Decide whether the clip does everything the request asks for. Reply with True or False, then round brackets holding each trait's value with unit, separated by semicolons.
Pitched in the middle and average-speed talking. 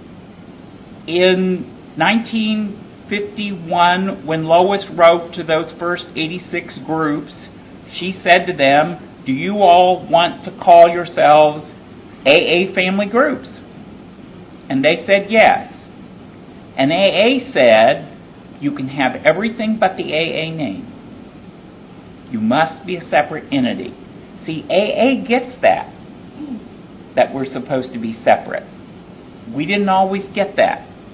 False (180 Hz; 115 wpm)